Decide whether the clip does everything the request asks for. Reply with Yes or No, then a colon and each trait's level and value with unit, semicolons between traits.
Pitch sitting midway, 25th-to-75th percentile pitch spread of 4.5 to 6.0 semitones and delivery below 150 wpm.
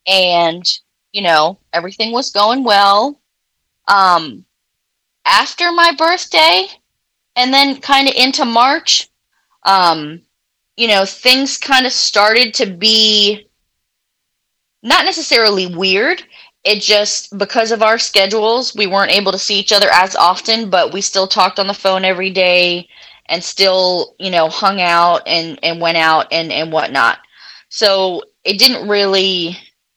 No: high, 200 Hz; average, 5.0 semitones; average, 140 wpm